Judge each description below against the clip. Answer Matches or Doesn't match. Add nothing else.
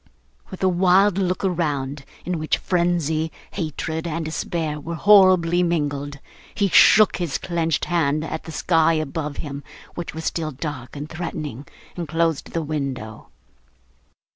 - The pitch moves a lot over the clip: Doesn't match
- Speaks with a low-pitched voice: Doesn't match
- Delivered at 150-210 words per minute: Doesn't match